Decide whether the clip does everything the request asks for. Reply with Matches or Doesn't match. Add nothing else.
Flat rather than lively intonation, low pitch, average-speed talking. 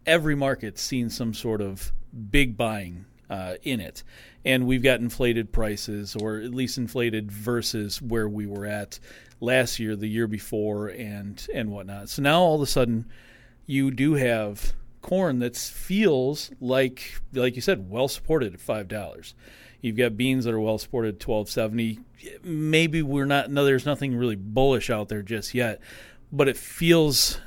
Doesn't match